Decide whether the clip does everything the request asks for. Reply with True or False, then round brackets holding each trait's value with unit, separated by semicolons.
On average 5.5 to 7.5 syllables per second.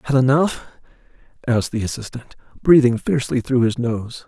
True (5.6 syllables/s)